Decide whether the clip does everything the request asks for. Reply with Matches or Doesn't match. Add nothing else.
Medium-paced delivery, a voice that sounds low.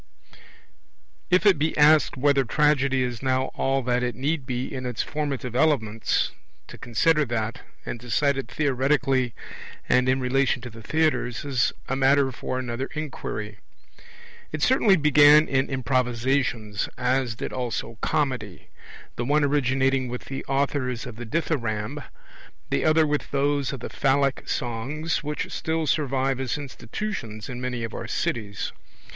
Matches